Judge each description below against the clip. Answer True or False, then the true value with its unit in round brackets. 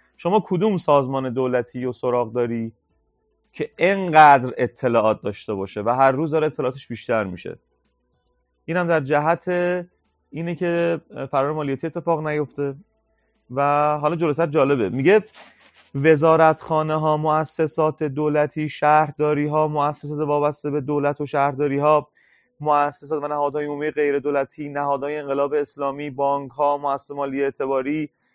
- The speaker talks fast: False (130 wpm)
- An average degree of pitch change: False (2.0 semitones)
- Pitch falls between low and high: True (145 Hz)